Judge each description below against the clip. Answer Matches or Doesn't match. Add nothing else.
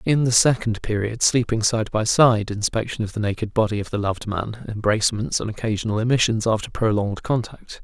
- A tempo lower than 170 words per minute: Doesn't match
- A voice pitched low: Matches